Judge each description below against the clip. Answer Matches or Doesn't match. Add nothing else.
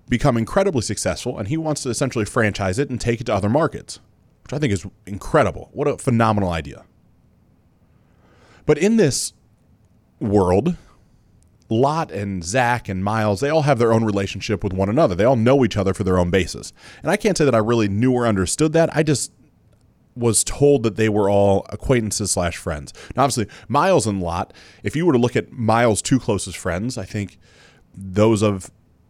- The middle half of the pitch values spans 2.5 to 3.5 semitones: Doesn't match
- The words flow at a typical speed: Matches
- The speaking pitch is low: Matches